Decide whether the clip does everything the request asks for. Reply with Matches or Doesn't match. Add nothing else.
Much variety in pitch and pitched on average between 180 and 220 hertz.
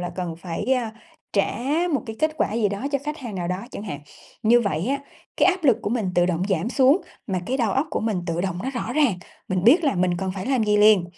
Matches